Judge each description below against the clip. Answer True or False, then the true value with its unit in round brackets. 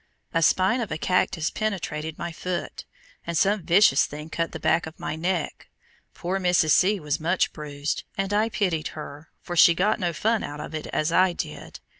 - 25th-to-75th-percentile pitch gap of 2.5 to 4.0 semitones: True (3.4 semitones)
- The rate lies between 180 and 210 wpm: True (195 wpm)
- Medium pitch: True (170 Hz)